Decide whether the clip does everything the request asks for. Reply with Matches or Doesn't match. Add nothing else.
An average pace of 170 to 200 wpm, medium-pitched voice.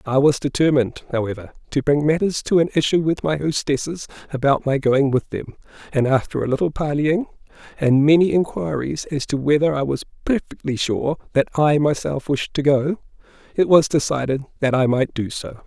Matches